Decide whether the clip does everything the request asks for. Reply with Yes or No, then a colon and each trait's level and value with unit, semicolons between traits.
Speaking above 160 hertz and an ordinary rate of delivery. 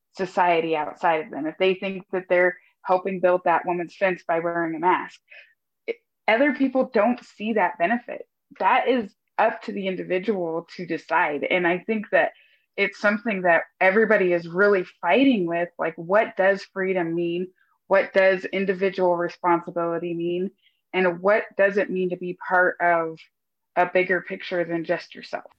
Yes: medium, 185 Hz; average, 165 wpm